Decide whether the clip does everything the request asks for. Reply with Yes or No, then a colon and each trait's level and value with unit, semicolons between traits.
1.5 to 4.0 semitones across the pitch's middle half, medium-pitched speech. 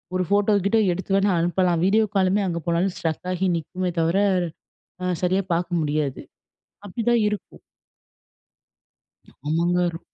Yes: narrow, 2.6 semitones; medium, 180 Hz